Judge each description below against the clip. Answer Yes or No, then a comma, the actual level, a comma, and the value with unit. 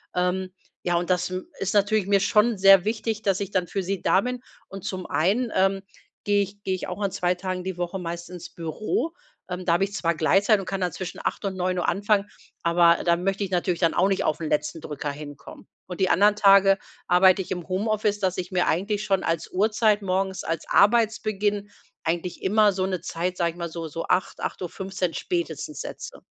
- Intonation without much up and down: Yes, narrow, 2.3 semitones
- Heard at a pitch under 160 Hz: No, medium, 185 Hz